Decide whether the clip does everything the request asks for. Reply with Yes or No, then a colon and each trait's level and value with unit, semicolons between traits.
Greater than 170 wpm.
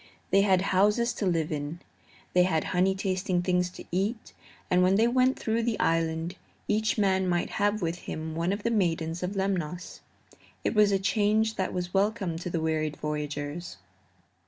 Yes: average, 180 wpm